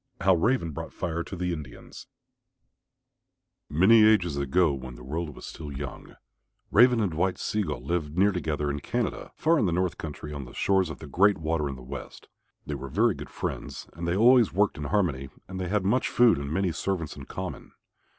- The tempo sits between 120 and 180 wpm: No, fast, 205 wpm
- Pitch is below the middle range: Yes, very low, 85 Hz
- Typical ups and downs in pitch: Yes, average, 4.9 semitones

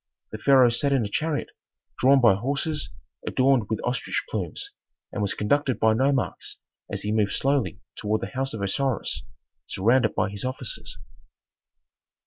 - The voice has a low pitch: Yes, low, 125 Hz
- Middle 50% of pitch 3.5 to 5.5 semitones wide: Yes, average, 4.3 semitones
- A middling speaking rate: Yes, average, 150 wpm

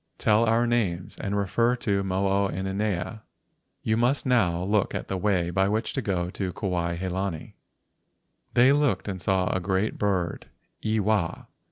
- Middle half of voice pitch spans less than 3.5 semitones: Yes, average, 2.9 semitones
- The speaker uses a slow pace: No, average, 160 wpm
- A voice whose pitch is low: Yes, low, 100 Hz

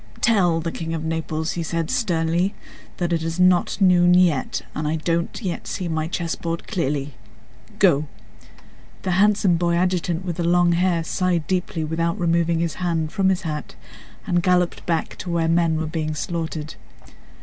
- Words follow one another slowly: No, average, 170 wpm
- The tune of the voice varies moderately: No, narrow, 1.7 semitones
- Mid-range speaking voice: Yes, medium, 170 Hz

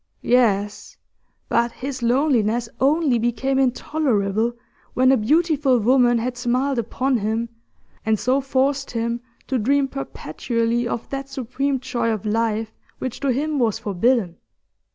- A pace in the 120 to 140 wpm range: Yes, slow, 135 wpm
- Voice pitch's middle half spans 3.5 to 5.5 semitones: No, average, 2.9 semitones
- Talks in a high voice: Yes, high, 245 Hz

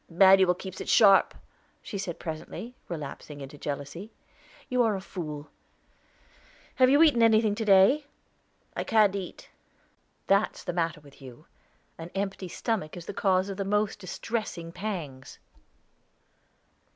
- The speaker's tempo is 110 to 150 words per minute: Yes, slow, 135 wpm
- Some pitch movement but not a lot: Yes, average, 4.5 semitones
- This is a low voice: No, high, 190 Hz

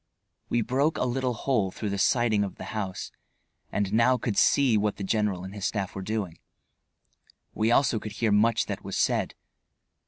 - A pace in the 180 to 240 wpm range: Yes, average, 185 wpm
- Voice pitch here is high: No, low, 110 Hz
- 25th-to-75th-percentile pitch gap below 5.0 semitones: Yes, average, 2.9 semitones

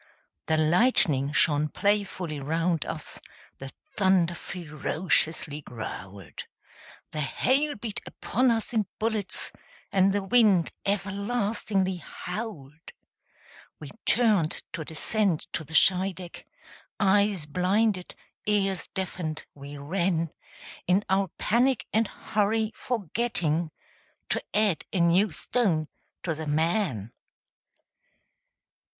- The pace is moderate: No, slow, 100 wpm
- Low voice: No, medium, 185 Hz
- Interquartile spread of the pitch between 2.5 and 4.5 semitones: No, average, 4.9 semitones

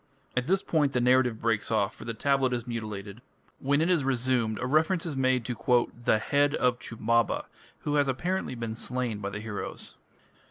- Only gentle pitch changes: No, average, 3.7 semitones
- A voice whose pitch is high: No, low, 125 Hz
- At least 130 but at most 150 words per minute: No, average, 190 wpm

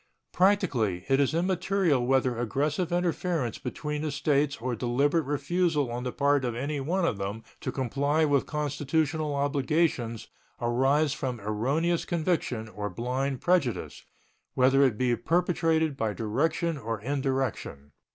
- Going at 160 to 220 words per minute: No, slow, 135 wpm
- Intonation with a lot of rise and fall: No, average, 4.6 semitones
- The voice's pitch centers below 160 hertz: Yes, medium, 140 Hz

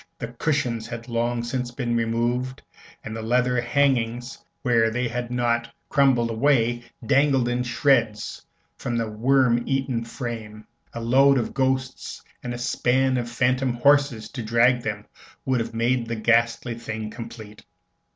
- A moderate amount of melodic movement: No, narrow, 1.8 semitones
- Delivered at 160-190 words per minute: No, average, 150 wpm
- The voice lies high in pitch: No, low, 120 Hz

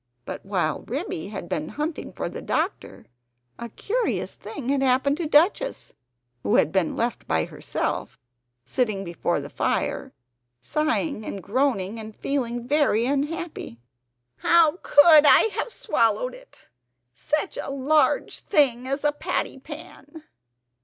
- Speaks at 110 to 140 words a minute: Yes, slow, 135 wpm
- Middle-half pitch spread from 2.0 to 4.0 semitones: No, average, 5.2 semitones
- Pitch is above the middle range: Yes, very high, 280 Hz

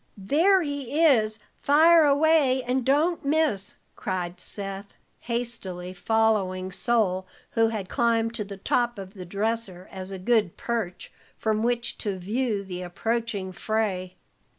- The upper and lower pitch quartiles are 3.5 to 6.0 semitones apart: Yes, average, 4.6 semitones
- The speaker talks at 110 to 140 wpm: Yes, slow, 135 wpm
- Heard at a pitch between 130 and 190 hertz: No, high, 220 Hz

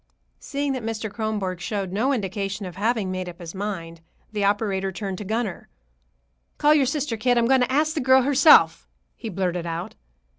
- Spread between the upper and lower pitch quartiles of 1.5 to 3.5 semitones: No, average, 5.1 semitones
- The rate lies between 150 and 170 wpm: No, average, 185 wpm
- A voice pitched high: Yes, high, 210 Hz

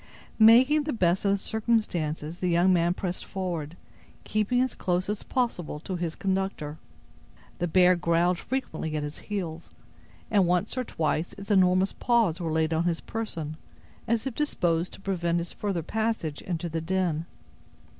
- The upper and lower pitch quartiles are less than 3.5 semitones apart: No, average, 4.0 semitones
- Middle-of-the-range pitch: Yes, medium, 180 Hz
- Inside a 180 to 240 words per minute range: No, average, 165 wpm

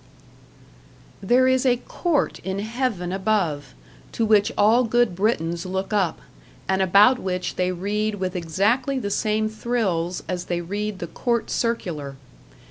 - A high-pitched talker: Yes, high, 205 Hz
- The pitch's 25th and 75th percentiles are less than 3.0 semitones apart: No, average, 4.2 semitones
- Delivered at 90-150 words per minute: Yes, average, 140 wpm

